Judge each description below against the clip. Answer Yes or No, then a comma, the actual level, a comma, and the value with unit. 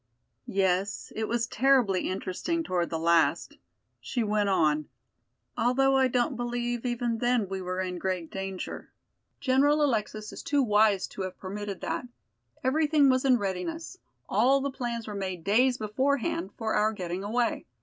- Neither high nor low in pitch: No, high, 220 Hz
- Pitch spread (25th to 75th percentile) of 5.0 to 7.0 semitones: Yes, average, 5.3 semitones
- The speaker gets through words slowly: No, average, 155 wpm